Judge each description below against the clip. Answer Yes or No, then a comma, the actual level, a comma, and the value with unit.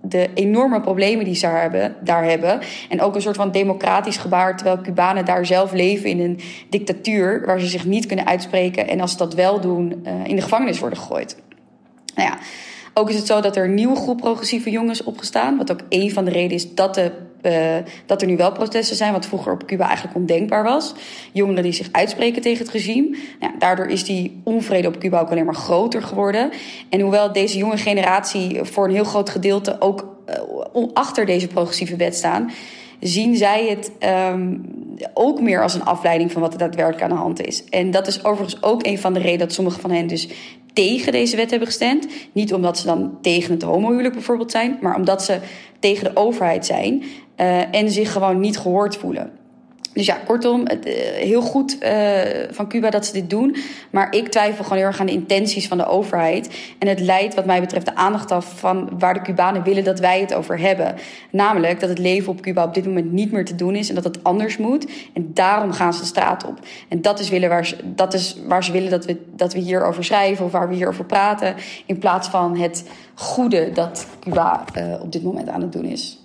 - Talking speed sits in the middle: No, fast, 220 wpm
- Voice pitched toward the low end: No, high, 195 Hz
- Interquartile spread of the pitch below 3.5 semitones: Yes, average, 2.9 semitones